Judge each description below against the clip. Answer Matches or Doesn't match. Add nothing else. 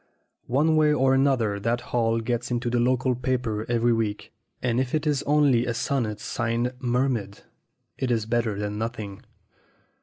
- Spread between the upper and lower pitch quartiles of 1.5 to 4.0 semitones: Matches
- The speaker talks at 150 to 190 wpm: Matches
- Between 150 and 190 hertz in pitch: Doesn't match